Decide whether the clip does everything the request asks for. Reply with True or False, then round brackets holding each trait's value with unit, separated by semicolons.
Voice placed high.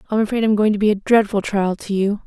True (210 Hz)